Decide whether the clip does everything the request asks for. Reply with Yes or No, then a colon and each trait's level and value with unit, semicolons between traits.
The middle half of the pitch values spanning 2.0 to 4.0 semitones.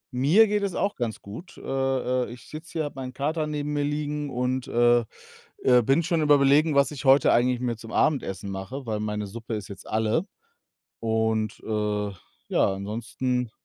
No: average, 4.8 semitones